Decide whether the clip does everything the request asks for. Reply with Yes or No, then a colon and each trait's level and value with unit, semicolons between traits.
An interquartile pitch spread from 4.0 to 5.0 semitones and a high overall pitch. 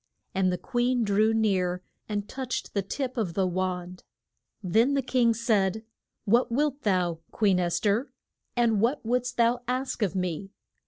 Yes: average, 4.6 semitones; high, 215 Hz